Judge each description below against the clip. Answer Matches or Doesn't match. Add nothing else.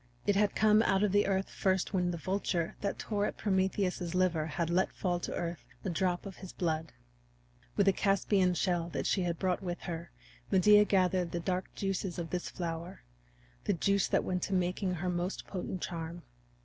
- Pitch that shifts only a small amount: Matches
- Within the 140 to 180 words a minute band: Doesn't match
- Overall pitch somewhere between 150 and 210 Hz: Matches